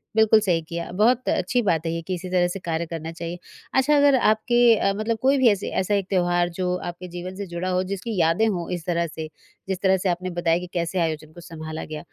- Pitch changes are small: No, average, 3.8 semitones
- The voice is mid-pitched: Yes, medium, 180 Hz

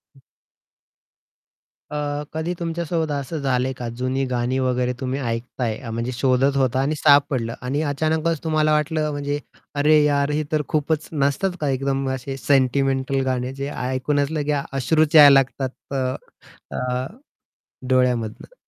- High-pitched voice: No, medium, 140 Hz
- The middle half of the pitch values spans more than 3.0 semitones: No, average, 2.7 semitones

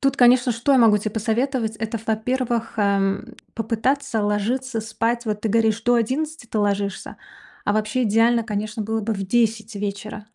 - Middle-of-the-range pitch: No, high, 225 Hz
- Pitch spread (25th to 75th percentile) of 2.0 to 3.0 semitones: Yes, narrow, 2.4 semitones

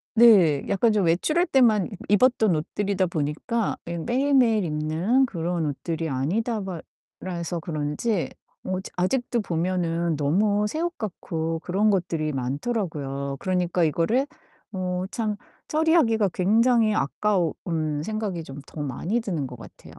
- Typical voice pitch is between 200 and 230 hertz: No, medium, 185 Hz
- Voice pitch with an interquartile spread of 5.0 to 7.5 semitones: Yes, wide, 5.5 semitones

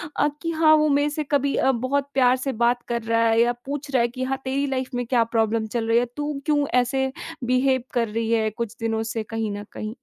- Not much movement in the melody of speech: No, average, 3.4 semitones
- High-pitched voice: Yes, very high, 250 Hz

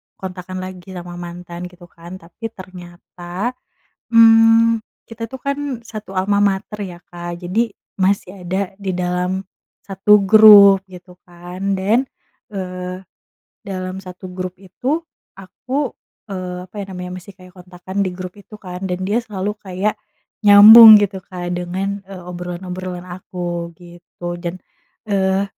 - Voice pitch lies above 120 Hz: Yes, medium, 185 Hz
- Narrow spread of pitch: Yes, narrow, 2.0 semitones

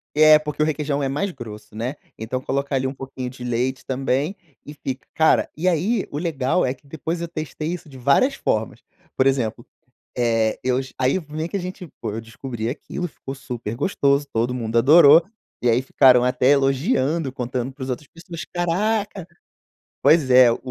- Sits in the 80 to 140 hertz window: Yes, low, 135 Hz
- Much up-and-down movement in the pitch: No, average, 3.9 semitones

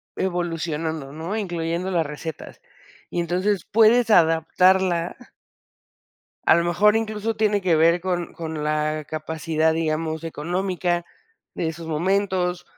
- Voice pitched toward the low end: No, medium, 170 Hz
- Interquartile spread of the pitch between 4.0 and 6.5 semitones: No, average, 2.8 semitones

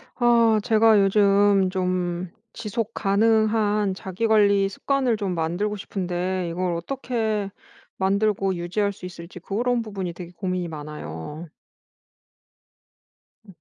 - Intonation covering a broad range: No, average, 3.2 semitones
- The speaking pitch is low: No, high, 195 Hz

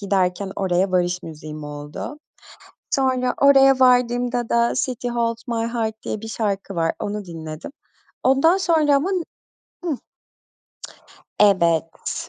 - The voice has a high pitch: Yes, high, 225 Hz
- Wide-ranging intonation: Yes, wide, 6.1 semitones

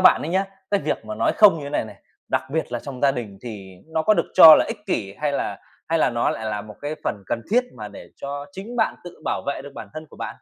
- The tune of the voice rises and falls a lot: Yes, wide, 7.9 semitones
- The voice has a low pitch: No, medium, 145 Hz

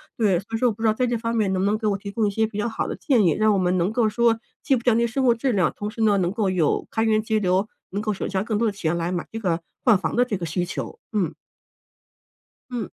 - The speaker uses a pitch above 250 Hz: No, high, 215 Hz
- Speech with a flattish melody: No, average, 3.2 semitones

